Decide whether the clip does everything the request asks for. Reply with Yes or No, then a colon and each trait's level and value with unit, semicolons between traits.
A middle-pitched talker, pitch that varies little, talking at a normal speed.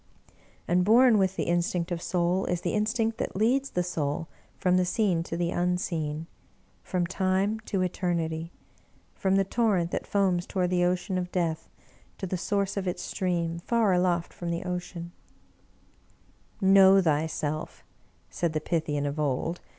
Yes: medium, 180 Hz; narrow, 2.3 semitones; average, 160 wpm